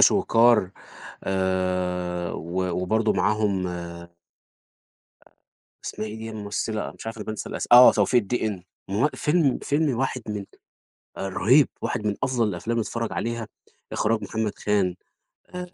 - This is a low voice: Yes, low, 105 Hz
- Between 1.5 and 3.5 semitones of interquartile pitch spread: No, average, 4.0 semitones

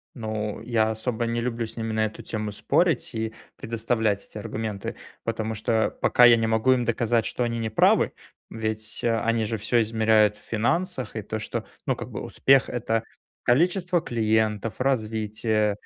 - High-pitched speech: No, low, 110 Hz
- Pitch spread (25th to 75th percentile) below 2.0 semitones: Yes, narrow, 1.5 semitones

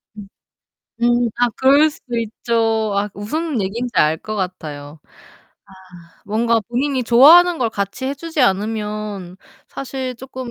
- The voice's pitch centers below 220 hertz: No, high, 230 Hz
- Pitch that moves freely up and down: No, average, 4.3 semitones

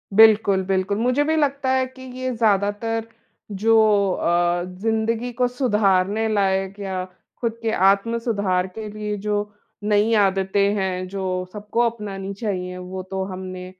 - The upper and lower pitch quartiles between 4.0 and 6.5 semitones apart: No, average, 3.0 semitones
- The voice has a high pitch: Yes, high, 205 Hz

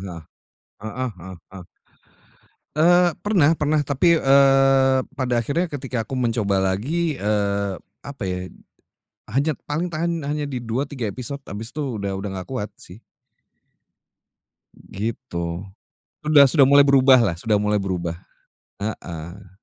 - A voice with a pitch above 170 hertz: No, low, 130 Hz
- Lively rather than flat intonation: Yes, wide, 6.1 semitones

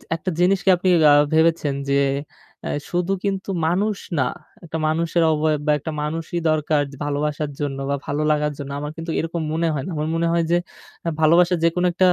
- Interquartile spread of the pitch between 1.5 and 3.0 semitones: Yes, narrow, 2.5 semitones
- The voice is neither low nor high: Yes, medium, 160 Hz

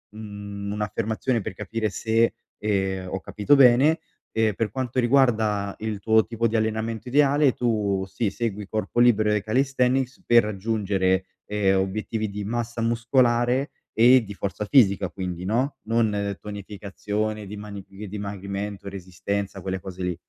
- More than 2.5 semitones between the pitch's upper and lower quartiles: Yes, average, 2.9 semitones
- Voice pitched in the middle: No, low, 105 Hz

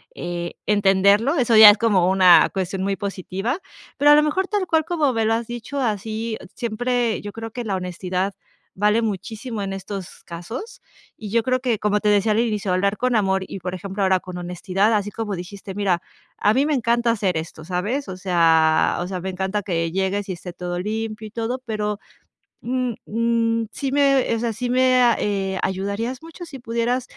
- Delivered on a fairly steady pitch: No, average, 3.7 semitones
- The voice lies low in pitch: No, high, 210 Hz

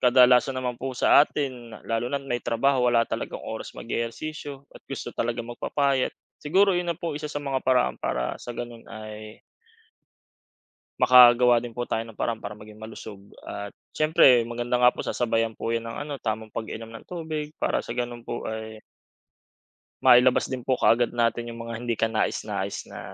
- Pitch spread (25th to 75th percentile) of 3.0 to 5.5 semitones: No, narrow, 2.6 semitones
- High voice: No, low, 120 Hz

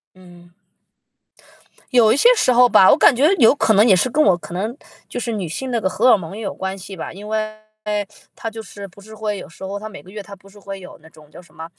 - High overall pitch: Yes, high, 205 Hz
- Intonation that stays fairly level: No, average, 3.1 semitones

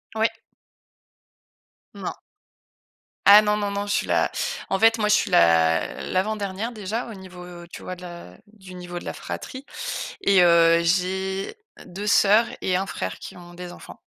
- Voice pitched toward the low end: No, high, 190 Hz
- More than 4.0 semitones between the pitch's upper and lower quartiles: No, average, 3.0 semitones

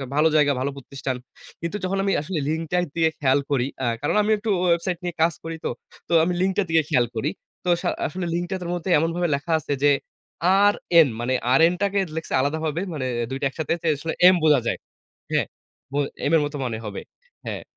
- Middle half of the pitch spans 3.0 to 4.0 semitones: Yes, average, 3.6 semitones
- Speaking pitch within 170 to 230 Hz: No, medium, 160 Hz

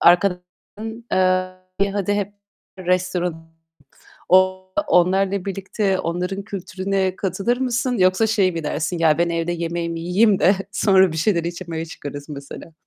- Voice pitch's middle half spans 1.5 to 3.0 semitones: Yes, average, 2.7 semitones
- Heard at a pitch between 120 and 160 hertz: No, medium, 185 Hz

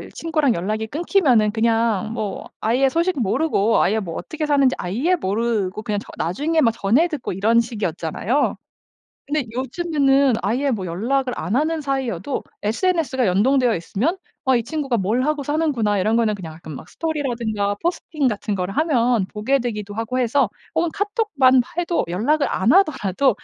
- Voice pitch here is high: Yes, high, 245 Hz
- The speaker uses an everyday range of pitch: No, wide, 5.8 semitones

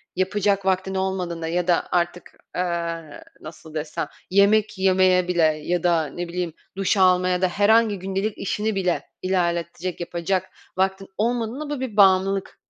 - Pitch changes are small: Yes, narrow, 2.2 semitones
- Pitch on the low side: No, medium, 185 Hz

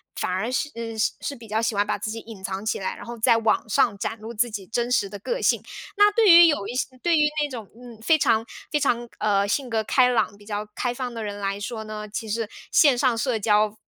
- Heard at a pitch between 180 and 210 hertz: No, high, 225 Hz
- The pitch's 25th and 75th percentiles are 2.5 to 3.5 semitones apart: Yes, average, 3.0 semitones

